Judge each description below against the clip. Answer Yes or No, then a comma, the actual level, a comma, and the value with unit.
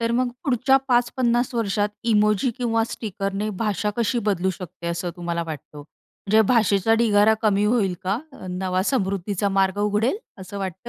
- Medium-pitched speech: No, high, 205 Hz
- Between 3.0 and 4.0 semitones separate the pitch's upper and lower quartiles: Yes, average, 3.4 semitones